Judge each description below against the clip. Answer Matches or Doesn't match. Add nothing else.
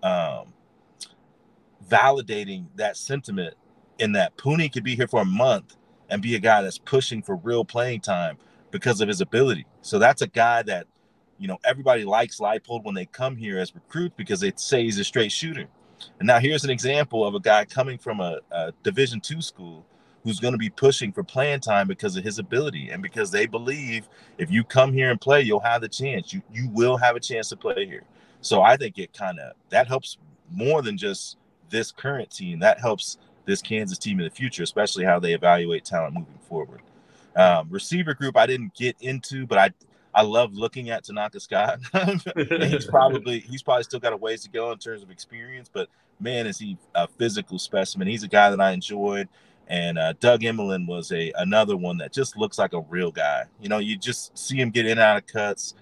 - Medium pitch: Doesn't match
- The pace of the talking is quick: Matches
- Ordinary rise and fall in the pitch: Doesn't match